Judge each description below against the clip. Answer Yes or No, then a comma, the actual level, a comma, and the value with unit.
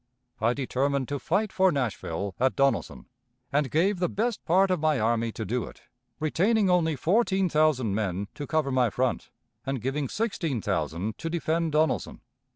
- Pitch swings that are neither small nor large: No, wide, 6.1 semitones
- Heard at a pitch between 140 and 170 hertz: Yes, medium, 145 Hz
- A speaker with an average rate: Yes, average, 165 wpm